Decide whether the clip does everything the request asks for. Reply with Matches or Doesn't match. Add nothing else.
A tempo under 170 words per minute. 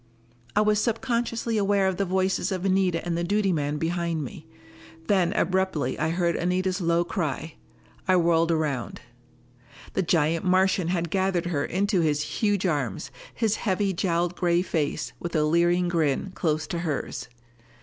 Matches